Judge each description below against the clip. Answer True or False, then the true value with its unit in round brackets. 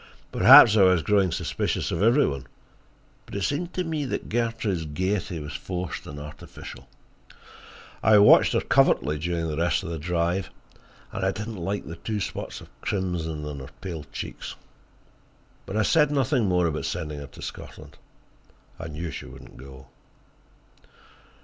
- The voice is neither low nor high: False (90 Hz)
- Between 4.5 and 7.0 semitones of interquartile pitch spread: True (5.0 semitones)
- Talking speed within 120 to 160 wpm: False (170 wpm)